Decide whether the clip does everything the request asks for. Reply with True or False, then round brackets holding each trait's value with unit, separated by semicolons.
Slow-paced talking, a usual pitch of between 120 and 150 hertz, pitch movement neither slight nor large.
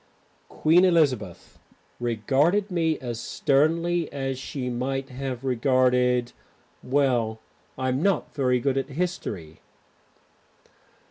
True (95 wpm; 135 Hz; 3.6 semitones)